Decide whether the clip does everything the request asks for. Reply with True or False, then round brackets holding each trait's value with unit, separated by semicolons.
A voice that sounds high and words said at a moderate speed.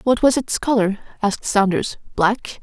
True (220 Hz; 160 wpm)